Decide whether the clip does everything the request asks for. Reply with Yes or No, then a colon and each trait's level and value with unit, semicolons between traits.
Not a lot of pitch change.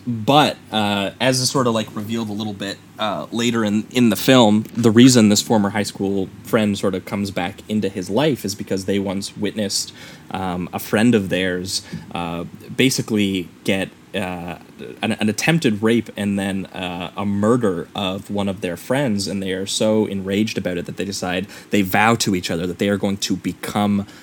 Yes: narrow, 2.2 semitones